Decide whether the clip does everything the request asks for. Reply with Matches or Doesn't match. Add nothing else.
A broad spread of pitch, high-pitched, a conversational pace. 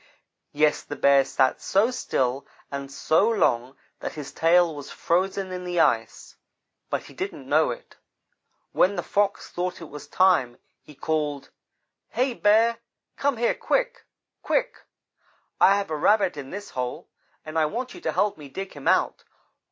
Doesn't match